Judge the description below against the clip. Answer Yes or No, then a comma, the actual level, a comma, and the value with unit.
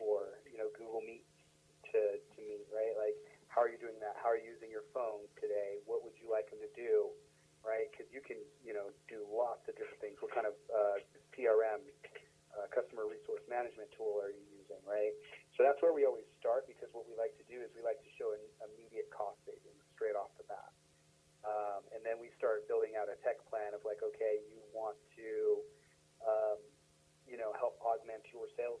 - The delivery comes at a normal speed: No, fast, 215 wpm